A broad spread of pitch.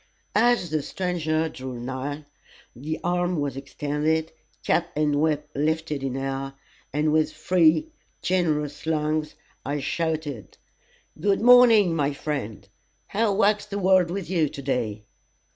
No: average, 3.8 semitones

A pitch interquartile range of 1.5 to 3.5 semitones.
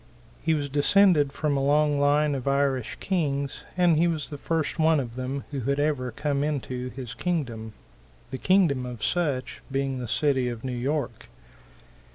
Yes: average, 3.0 semitones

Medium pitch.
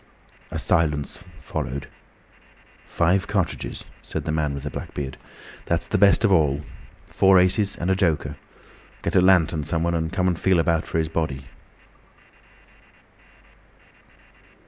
No: very low, 80 Hz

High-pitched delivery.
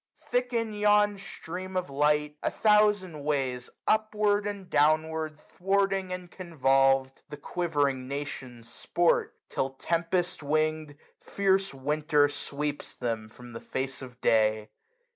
No: medium, 155 Hz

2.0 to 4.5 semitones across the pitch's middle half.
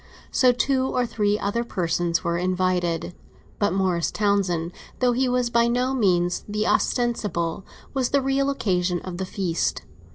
No: wide, 5.6 semitones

